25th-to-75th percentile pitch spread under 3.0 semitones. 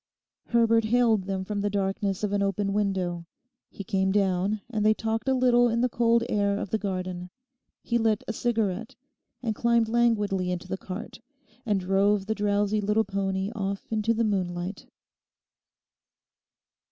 Yes: narrow, 2.5 semitones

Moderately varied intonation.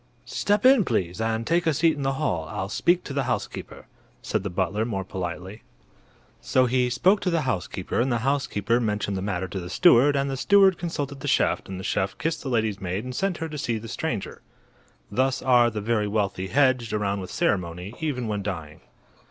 No: wide, 6.1 semitones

